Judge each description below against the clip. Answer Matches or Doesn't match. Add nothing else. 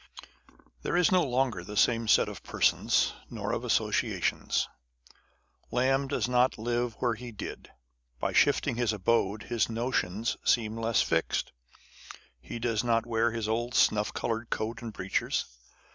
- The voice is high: Doesn't match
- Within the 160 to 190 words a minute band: Doesn't match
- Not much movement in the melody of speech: Matches